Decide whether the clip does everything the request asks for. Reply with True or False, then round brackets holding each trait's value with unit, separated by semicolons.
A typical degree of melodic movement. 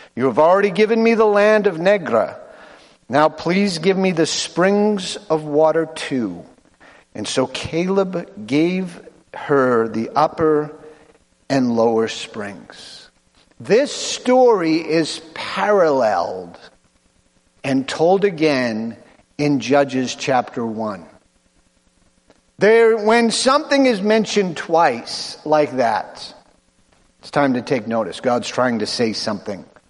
False (7.5 semitones)